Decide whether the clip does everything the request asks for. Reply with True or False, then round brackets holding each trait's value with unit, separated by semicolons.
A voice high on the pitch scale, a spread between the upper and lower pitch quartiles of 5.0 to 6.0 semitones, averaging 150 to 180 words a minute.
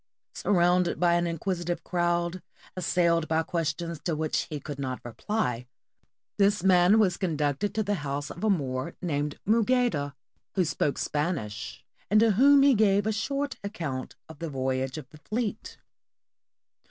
False (175 Hz; 5.6 semitones; 155 wpm)